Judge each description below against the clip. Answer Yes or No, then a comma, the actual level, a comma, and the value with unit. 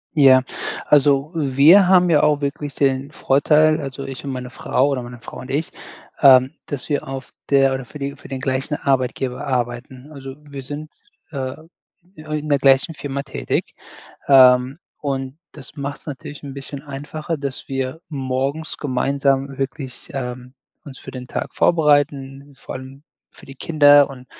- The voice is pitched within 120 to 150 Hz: Yes, medium, 140 Hz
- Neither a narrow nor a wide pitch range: No, narrow, 1.8 semitones